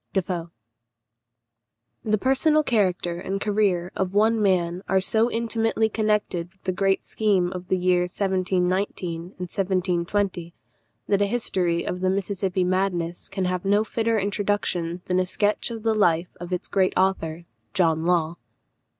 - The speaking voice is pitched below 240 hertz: Yes, high, 190 Hz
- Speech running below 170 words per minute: Yes, average, 150 wpm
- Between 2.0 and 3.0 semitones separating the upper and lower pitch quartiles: Yes, narrow, 2.6 semitones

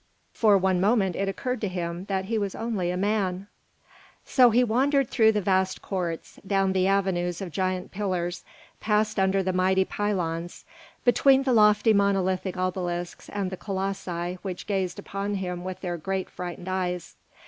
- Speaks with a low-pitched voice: No, high, 190 Hz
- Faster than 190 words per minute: No, average, 165 wpm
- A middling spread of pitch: No, narrow, 2.3 semitones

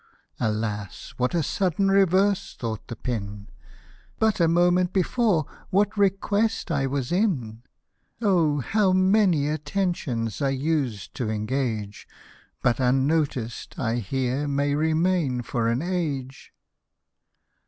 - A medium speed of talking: No, slow, 125 wpm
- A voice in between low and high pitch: Yes, medium, 145 Hz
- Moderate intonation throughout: No, wide, 7.2 semitones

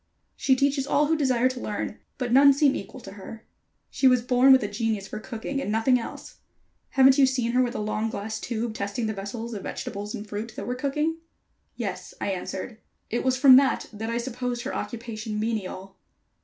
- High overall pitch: Yes, high, 235 Hz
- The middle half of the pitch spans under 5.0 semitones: Yes, average, 3.5 semitones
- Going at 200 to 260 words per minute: Yes, fast, 205 wpm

